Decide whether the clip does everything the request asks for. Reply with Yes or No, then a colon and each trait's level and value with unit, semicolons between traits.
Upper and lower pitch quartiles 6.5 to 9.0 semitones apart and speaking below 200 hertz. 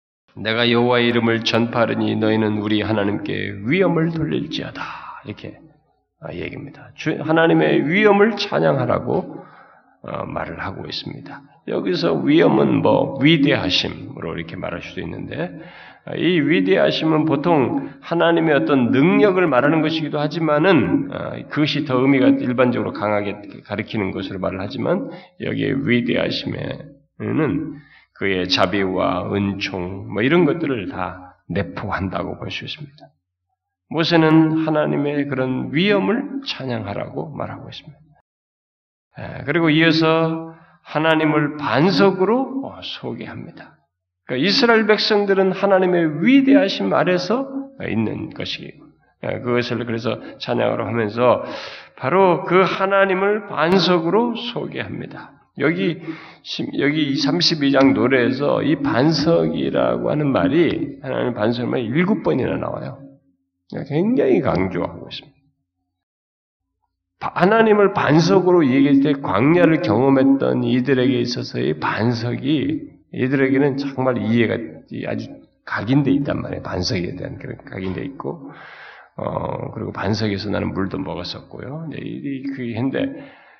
Yes: wide, 7.2 semitones; medium, 140 Hz